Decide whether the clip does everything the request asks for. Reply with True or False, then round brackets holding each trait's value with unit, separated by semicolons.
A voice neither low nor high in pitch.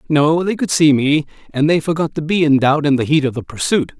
True (150 Hz)